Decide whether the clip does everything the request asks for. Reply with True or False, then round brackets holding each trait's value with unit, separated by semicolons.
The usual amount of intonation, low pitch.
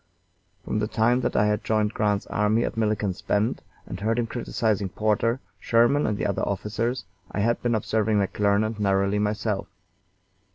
False (1.8 semitones; 105 Hz)